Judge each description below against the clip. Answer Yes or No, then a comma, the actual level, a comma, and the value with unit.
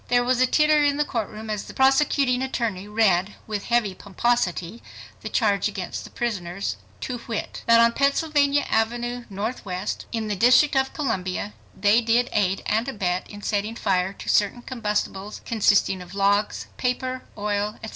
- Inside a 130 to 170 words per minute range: Yes, average, 165 wpm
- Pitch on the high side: Yes, high, 220 Hz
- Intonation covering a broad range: No, average, 3.6 semitones